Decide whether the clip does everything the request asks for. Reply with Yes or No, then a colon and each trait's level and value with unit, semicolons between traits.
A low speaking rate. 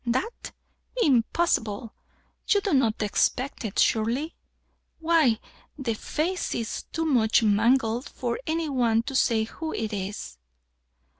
Yes: slow, 125 wpm